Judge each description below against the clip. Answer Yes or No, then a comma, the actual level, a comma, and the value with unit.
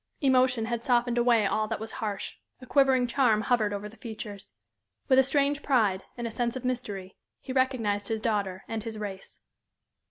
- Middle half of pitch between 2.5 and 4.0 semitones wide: Yes, average, 3.3 semitones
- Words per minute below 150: No, average, 185 wpm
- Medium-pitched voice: No, high, 230 Hz